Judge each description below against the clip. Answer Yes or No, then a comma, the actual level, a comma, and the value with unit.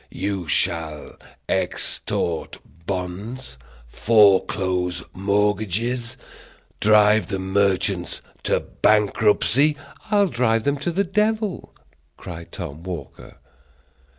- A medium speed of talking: No, slow, 90 wpm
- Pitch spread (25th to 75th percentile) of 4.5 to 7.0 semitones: Yes, average, 5.0 semitones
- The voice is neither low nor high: No, low, 105 Hz